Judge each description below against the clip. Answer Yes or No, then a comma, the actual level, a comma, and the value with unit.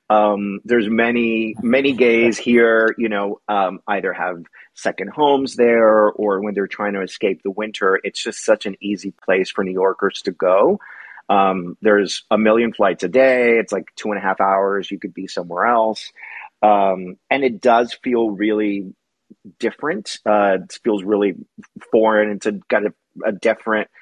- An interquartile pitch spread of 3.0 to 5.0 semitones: No, narrow, 2.5 semitones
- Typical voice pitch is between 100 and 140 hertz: Yes, low, 105 Hz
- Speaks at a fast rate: No, average, 175 wpm